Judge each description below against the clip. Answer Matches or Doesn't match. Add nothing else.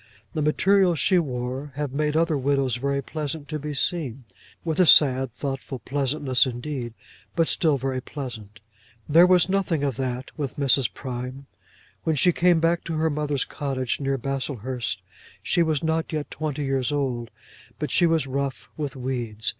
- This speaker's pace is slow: Doesn't match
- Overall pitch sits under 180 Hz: Matches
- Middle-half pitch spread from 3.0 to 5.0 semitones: Matches